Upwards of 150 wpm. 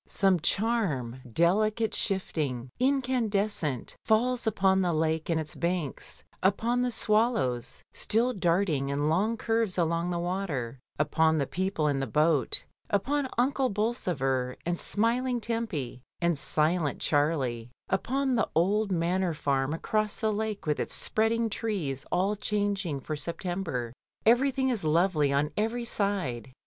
No: slow, 135 wpm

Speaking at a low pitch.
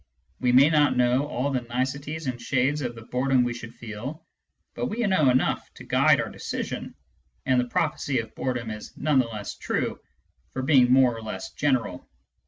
Yes: low, 130 Hz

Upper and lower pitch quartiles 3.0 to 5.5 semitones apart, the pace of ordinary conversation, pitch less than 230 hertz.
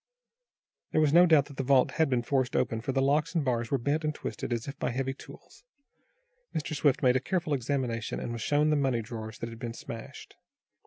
No: average, 3.9 semitones; fast, 225 wpm; low, 135 Hz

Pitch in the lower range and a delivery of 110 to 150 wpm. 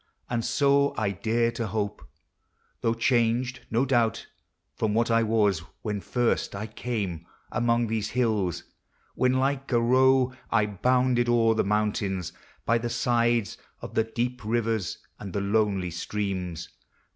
Yes: low, 115 Hz; average, 145 wpm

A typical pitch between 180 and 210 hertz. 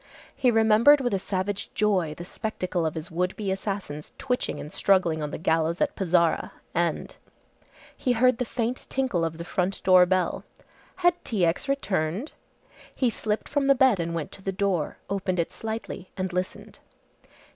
Yes: high, 190 Hz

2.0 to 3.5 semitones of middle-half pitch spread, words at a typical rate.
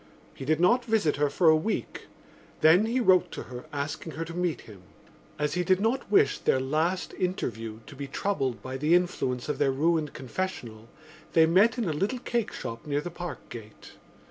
No: wide, 5.6 semitones; average, 190 wpm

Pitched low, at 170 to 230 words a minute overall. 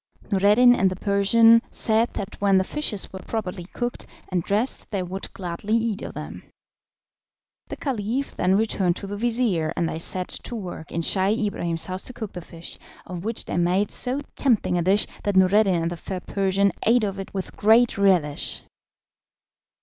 No: high, 200 Hz; average, 180 wpm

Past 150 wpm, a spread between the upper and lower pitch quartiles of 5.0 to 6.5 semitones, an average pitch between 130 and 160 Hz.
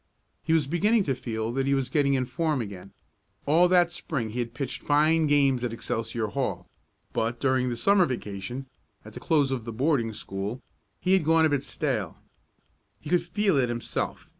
Yes: average, 190 wpm; average, 5.3 semitones; low, 135 Hz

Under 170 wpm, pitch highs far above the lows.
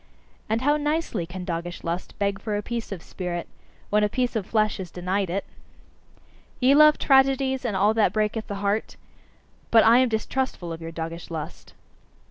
No: average, 180 wpm; wide, 5.7 semitones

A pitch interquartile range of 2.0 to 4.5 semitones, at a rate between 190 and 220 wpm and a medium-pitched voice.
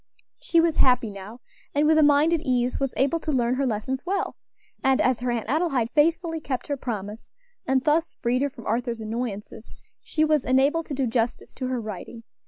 No: average, 4.2 semitones; average, 200 wpm; very high, 260 Hz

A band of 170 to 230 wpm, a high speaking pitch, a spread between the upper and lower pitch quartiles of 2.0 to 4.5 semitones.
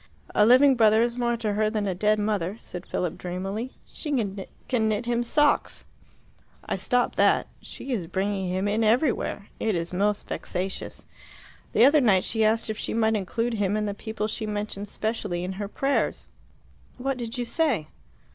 Yes: average, 180 wpm; high, 215 Hz; average, 3.1 semitones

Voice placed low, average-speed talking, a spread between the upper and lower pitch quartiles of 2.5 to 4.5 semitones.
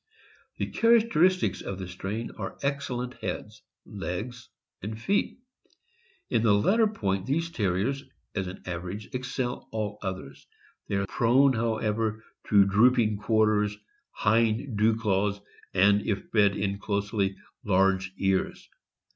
No: low, 105 Hz; slow, 125 wpm; average, 3.7 semitones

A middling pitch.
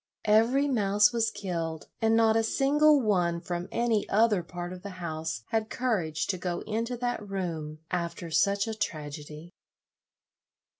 No: high, 200 Hz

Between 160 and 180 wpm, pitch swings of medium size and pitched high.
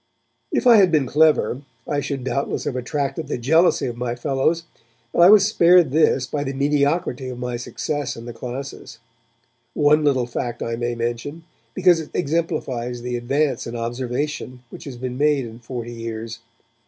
No: average, 175 wpm; average, 3.9 semitones; low, 135 Hz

